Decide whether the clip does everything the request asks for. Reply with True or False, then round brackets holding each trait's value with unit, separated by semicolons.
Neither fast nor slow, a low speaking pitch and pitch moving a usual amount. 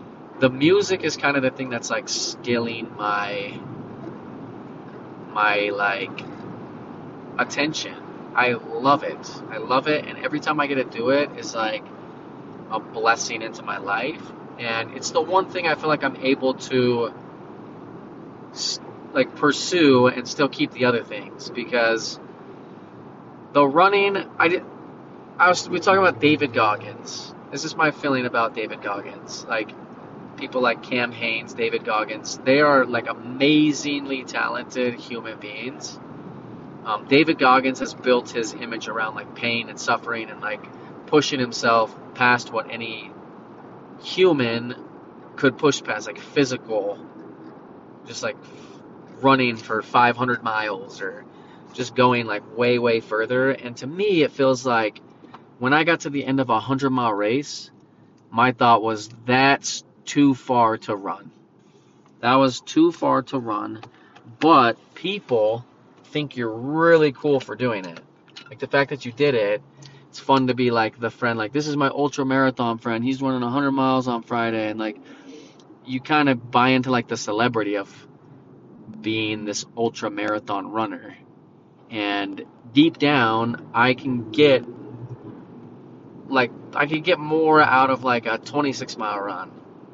True (150 wpm; 125 Hz; 3.8 semitones)